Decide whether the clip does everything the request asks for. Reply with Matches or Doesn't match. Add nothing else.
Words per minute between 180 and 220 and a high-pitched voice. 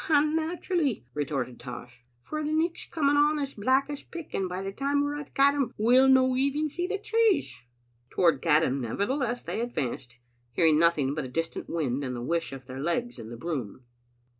Matches